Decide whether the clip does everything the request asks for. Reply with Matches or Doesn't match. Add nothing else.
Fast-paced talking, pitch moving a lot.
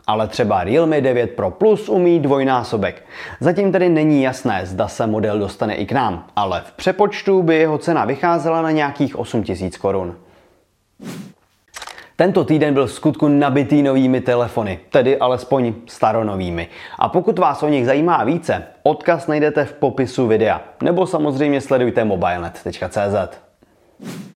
Doesn't match